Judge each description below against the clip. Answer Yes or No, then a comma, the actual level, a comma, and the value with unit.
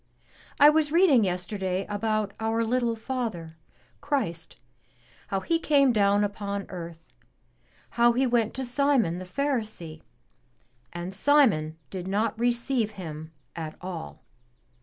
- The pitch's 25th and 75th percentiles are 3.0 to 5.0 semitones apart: No, wide, 5.6 semitones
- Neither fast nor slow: No, slow, 120 wpm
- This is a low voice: No, high, 215 Hz